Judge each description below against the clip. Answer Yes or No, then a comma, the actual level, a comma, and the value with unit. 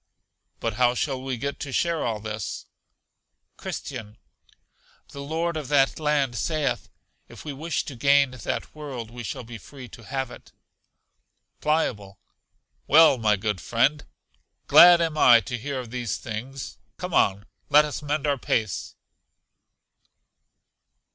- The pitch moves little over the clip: No, average, 4.3 semitones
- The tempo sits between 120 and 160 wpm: Yes, average, 140 wpm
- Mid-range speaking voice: No, low, 130 Hz